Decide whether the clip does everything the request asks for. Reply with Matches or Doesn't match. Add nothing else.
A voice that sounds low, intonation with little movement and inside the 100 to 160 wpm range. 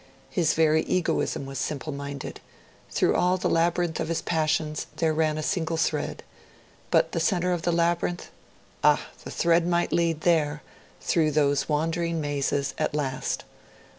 Doesn't match